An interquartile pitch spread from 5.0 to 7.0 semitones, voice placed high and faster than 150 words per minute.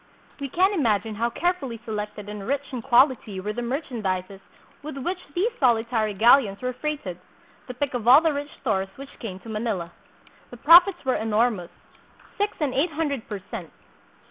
Yes: average, 5.3 semitones; high, 240 Hz; average, 170 wpm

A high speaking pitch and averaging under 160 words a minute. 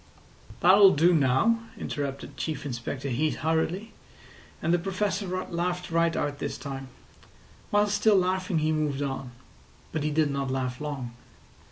No: medium, 155 Hz; average, 145 wpm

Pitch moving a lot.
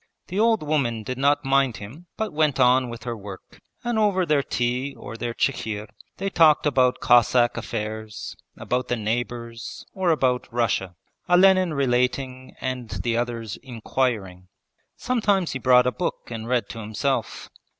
No: average, 4.2 semitones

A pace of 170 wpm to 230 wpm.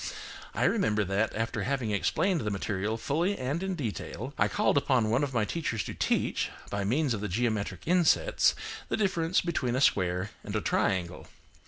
Yes: average, 180 wpm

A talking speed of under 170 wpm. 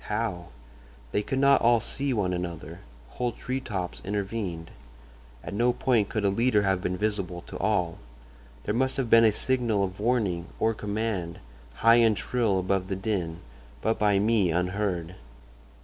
Yes: average, 160 wpm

